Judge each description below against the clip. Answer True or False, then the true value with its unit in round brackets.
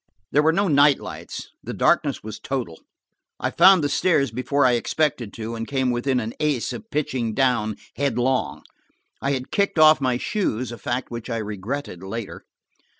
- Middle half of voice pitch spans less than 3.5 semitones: False (3.9 semitones)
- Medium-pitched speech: False (130 Hz)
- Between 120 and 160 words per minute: False (170 wpm)